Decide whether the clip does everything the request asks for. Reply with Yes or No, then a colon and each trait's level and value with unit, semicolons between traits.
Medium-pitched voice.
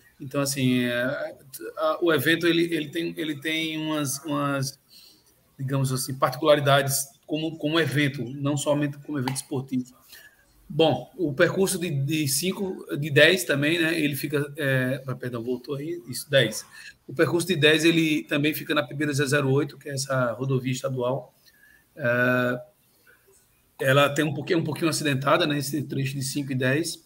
Yes: medium, 145 Hz